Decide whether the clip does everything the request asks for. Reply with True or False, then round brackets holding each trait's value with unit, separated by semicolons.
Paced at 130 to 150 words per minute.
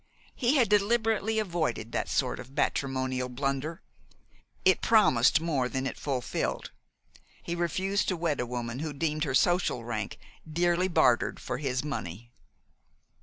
True (140 wpm)